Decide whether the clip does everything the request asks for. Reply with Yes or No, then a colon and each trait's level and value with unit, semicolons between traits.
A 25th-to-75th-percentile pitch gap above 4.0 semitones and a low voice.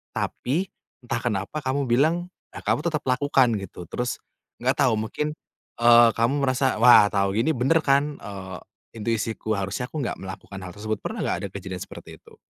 Yes: average, 5.2 semitones; low, 120 Hz